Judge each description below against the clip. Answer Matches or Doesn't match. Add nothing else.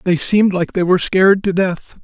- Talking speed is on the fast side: Matches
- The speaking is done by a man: Matches